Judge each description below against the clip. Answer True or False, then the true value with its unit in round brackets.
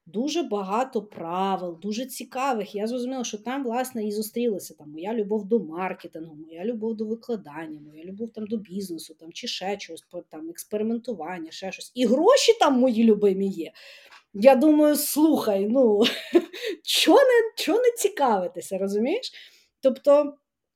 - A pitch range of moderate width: False (5.9 semitones)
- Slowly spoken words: False (135 wpm)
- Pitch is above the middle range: True (225 Hz)